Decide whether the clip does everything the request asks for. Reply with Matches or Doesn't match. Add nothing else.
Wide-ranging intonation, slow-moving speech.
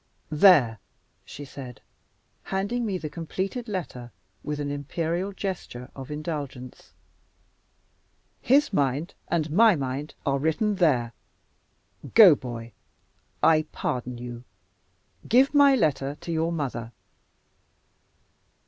Matches